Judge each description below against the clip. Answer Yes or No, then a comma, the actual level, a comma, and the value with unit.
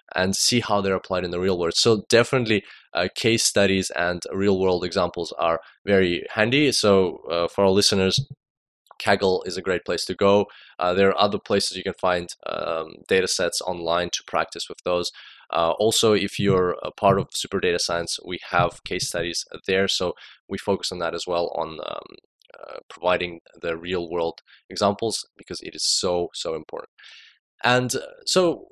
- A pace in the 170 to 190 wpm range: Yes, average, 180 wpm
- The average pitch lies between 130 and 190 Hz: No, very low, 95 Hz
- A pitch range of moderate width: Yes, average, 3.2 semitones